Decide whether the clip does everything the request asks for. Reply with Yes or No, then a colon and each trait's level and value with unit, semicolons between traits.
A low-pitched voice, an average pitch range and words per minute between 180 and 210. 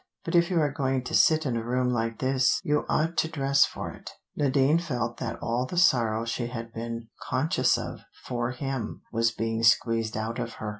Yes: low, 125 Hz; average, 3.3 semitones; fast, 205 wpm